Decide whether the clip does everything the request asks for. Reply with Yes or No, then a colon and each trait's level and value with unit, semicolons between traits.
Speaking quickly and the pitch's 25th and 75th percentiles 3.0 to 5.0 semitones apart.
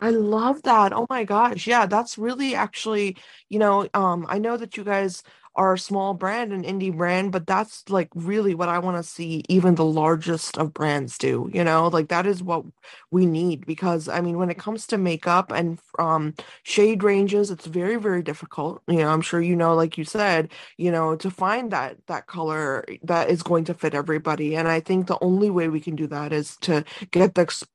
Yes: fast, 220 wpm; average, 3.7 semitones